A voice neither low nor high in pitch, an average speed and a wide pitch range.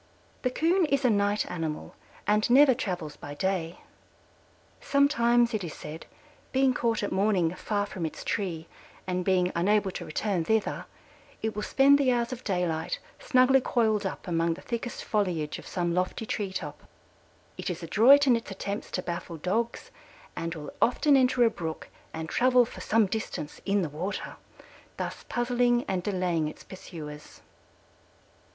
No: high, 200 Hz; average, 160 wpm; wide, 5.8 semitones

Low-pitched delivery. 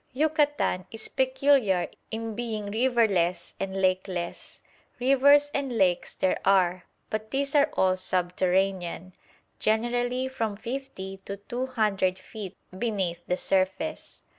No: high, 215 Hz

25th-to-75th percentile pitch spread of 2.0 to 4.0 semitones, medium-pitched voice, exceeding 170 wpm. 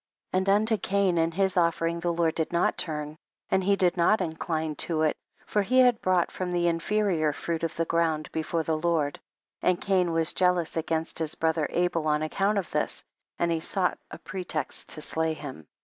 Yes: narrow, 2.6 semitones; medium, 170 Hz; fast, 205 wpm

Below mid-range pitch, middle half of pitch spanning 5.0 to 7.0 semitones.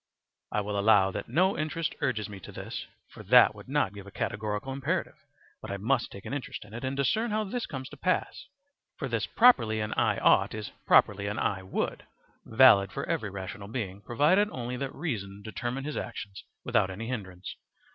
Yes: low, 115 Hz; wide, 5.6 semitones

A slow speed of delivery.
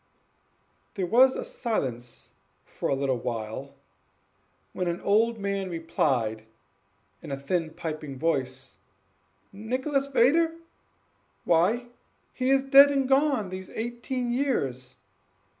Yes: slow, 110 wpm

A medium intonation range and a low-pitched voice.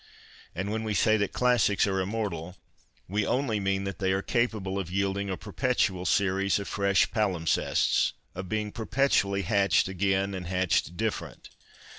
No: narrow, 2.1 semitones; low, 100 Hz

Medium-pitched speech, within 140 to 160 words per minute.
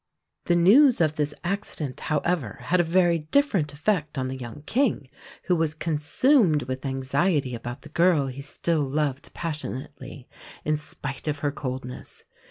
Yes: medium, 150 Hz; average, 155 wpm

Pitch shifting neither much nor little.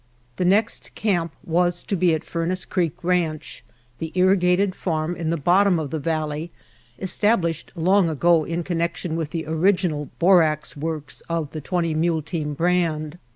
No: narrow, 2.3 semitones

